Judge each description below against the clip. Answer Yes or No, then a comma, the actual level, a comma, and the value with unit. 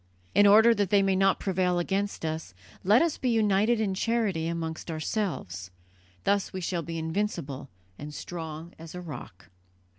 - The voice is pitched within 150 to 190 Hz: Yes, medium, 185 Hz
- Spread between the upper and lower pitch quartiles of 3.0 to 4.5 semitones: Yes, average, 4.1 semitones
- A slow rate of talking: No, average, 160 wpm